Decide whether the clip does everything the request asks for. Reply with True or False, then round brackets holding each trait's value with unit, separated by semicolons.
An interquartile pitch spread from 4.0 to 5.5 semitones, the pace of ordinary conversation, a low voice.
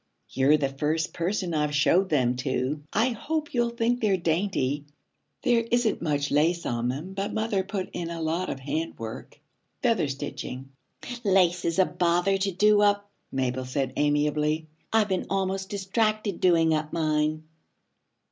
False (5.2 semitones; 155 wpm; 170 Hz)